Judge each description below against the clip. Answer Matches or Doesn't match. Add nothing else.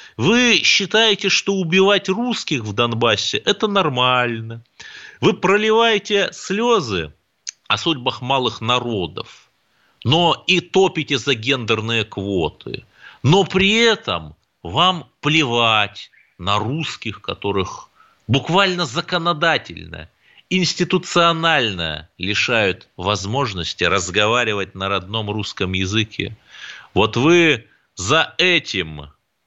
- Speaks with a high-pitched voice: Doesn't match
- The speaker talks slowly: Matches